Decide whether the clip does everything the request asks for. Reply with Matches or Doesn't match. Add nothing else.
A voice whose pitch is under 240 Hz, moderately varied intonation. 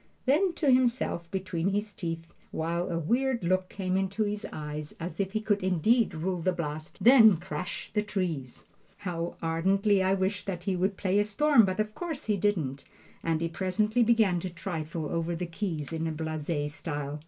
Matches